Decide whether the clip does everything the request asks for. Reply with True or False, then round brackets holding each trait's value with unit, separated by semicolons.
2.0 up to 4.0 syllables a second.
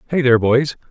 False (6.9 syllables/s)